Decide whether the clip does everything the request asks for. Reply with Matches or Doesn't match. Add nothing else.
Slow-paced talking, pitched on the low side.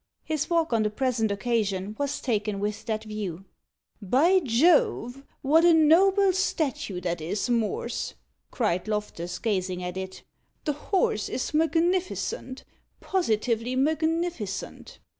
Doesn't match